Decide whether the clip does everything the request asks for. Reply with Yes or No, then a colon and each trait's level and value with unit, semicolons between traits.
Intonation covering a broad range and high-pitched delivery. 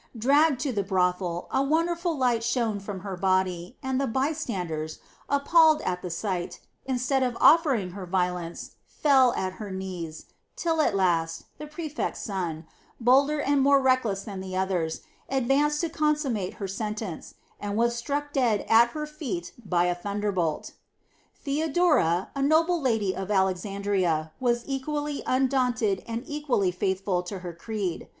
Yes: wide, 6.9 semitones; high, 220 Hz